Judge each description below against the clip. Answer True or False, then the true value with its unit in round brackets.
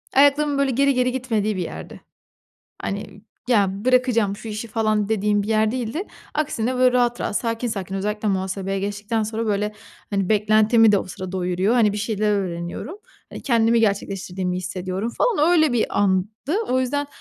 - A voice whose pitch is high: True (215 Hz)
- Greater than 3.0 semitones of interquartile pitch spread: True (3.6 semitones)